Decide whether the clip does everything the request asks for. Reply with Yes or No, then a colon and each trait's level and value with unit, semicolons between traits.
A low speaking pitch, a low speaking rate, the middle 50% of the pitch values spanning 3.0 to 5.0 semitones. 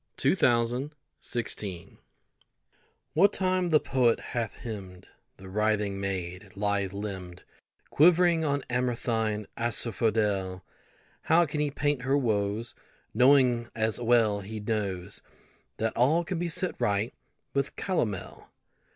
No: low, 115 Hz; slow, 115 wpm; wide, 5.5 semitones